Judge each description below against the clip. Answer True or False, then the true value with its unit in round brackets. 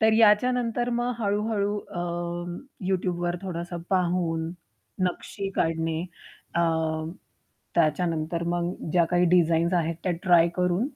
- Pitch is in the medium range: True (175 Hz)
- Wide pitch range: False (2.9 semitones)